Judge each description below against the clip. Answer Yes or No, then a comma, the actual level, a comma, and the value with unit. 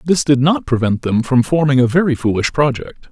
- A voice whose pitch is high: No, low, 135 Hz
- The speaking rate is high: Yes, fast, 210 wpm